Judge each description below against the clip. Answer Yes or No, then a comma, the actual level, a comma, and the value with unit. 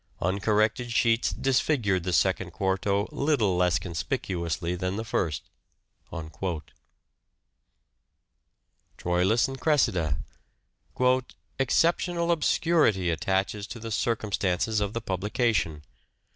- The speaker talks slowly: Yes, slow, 100 wpm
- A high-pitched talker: No, low, 100 Hz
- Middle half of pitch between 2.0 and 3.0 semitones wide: No, average, 4.9 semitones